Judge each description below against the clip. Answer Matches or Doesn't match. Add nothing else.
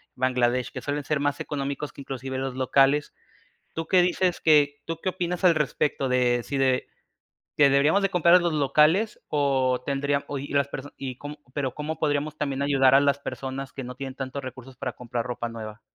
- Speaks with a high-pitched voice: Doesn't match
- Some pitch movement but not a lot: Doesn't match